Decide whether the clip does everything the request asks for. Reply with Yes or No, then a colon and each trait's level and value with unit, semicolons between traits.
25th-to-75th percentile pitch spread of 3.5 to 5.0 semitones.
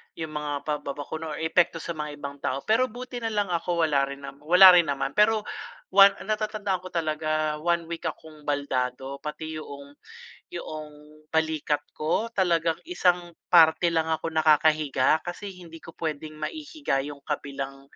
No: average, 3.1 semitones